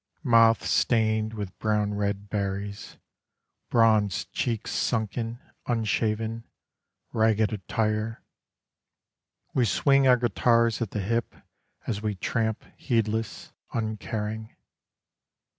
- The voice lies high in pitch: No, low, 110 Hz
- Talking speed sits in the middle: No, slow, 90 wpm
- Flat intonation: Yes, narrow, 1.6 semitones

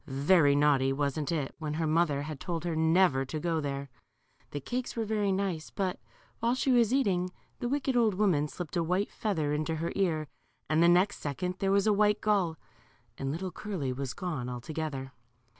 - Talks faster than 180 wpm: Yes, average, 190 wpm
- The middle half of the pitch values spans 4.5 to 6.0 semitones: Yes, average, 5.2 semitones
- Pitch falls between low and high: Yes, medium, 165 Hz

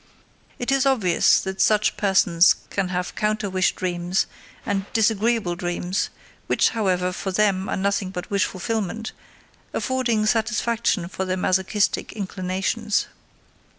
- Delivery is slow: Yes, slow, 125 wpm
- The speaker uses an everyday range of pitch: Yes, average, 3.0 semitones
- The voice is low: No, high, 195 Hz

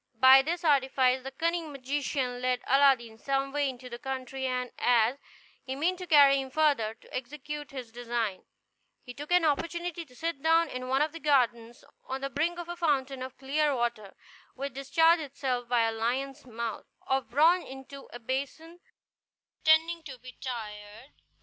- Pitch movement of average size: Yes, average, 3.2 semitones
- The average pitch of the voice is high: Yes, very high, 270 Hz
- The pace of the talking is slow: No, average, 175 wpm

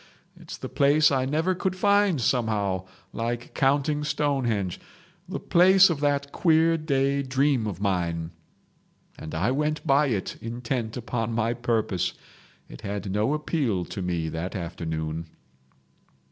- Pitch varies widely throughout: Yes, wide, 7.1 semitones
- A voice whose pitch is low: Yes, low, 120 Hz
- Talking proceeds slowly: Yes, slow, 130 wpm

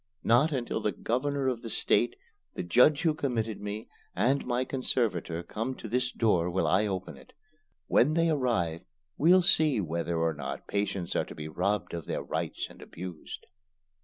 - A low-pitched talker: Yes, low, 110 Hz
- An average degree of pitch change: No, wide, 6.8 semitones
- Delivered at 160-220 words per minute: Yes, average, 175 wpm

